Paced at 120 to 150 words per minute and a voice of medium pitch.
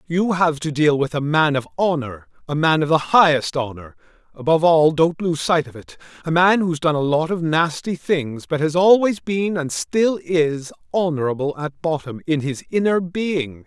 No: average, 190 wpm; medium, 160 Hz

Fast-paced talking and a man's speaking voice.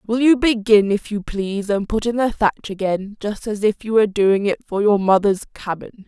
No: fast, 225 wpm; female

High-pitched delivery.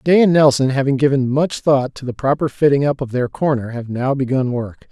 No: low, 135 Hz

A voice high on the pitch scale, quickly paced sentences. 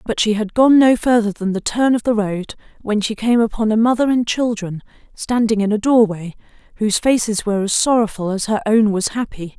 Yes: high, 220 Hz; fast, 215 wpm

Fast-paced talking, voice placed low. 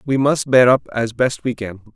Yes: fast, 245 wpm; low, 125 Hz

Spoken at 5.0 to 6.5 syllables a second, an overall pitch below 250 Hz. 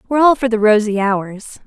Yes: 5.6 syllables/s; high, 225 Hz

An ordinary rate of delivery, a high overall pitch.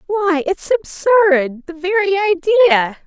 No: slow, 115 wpm; very high, 360 Hz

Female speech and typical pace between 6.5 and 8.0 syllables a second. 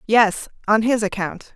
No: female; 4.1 syllables/s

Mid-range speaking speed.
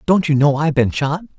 No: fast, 260 wpm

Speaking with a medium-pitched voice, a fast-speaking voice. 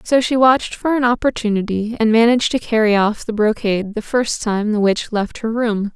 No: high, 225 Hz; fast, 210 wpm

